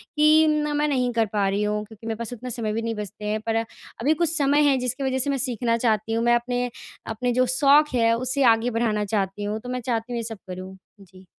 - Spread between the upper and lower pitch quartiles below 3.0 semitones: No, average, 3.4 semitones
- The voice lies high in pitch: Yes, high, 235 Hz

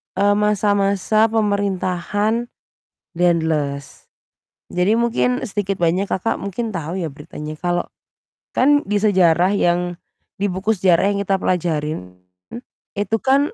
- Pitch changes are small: No, average, 3.3 semitones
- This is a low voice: No, high, 195 Hz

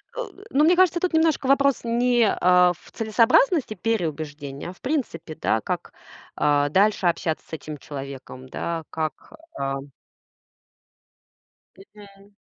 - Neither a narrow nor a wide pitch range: No, wide, 8.5 semitones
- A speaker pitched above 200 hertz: No, high, 190 Hz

